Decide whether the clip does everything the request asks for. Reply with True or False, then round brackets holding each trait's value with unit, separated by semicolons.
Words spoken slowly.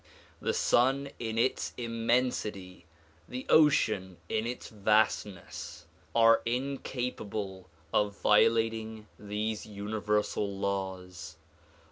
True (85 wpm)